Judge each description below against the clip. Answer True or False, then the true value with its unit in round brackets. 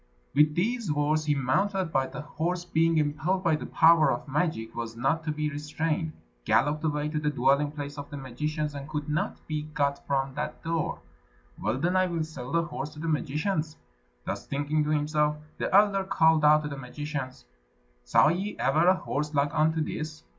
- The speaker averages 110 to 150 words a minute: False (195 wpm)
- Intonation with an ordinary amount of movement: False (2.0 semitones)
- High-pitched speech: False (150 Hz)